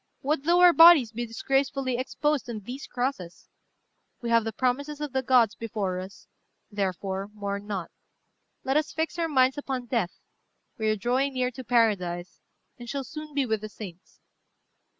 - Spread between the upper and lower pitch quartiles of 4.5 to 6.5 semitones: Yes, average, 4.8 semitones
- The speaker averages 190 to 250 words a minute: No, average, 170 wpm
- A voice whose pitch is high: Yes, high, 245 Hz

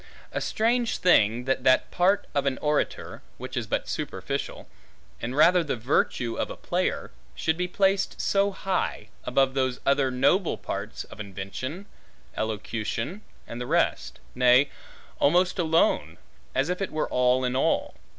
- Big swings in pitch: Yes, wide, 6.3 semitones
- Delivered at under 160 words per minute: Yes, average, 150 wpm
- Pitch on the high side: No, medium, 140 Hz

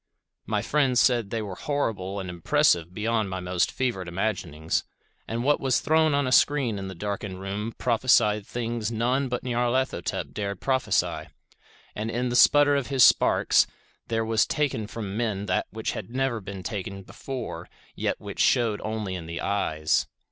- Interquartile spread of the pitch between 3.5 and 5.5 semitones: Yes, average, 4.5 semitones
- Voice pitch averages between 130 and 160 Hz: No, low, 110 Hz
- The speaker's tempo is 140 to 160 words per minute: No, average, 170 wpm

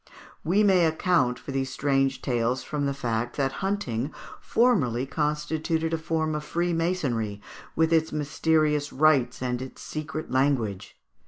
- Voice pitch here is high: No, medium, 150 Hz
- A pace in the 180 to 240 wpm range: No, average, 140 wpm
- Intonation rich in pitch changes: No, average, 3.9 semitones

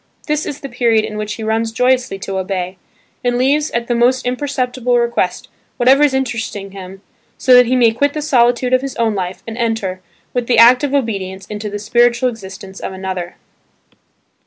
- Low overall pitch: No, high, 235 Hz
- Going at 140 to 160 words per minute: No, average, 190 wpm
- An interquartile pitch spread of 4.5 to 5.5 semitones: No, average, 3.8 semitones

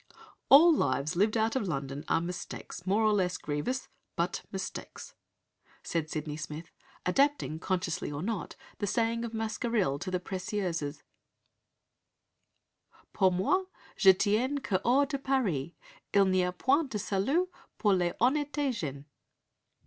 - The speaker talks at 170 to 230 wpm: No, average, 140 wpm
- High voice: Yes, high, 195 Hz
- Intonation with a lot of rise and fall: Yes, wide, 5.8 semitones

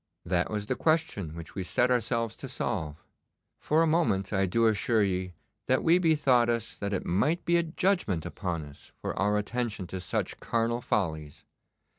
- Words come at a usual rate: Yes, average, 180 wpm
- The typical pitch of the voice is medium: No, low, 110 Hz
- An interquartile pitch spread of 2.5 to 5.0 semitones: No, wide, 5.6 semitones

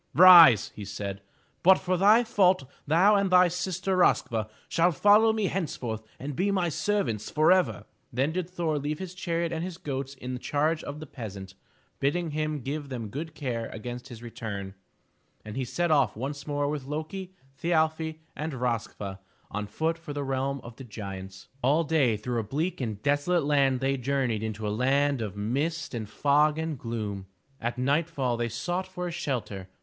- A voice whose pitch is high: No, medium, 140 Hz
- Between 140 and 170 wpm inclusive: No, average, 185 wpm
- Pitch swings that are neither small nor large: No, wide, 6.1 semitones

